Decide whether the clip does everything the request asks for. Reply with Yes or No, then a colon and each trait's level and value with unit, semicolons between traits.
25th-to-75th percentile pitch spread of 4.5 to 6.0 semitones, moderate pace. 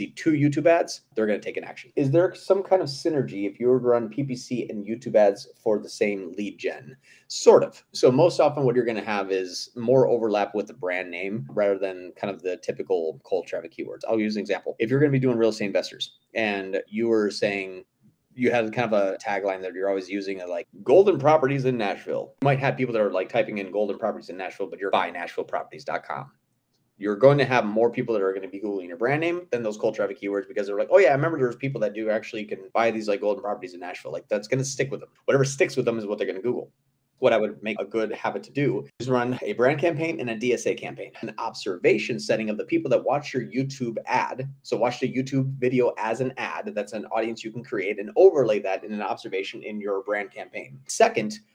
No: average, 5.0 semitones; fast, 255 wpm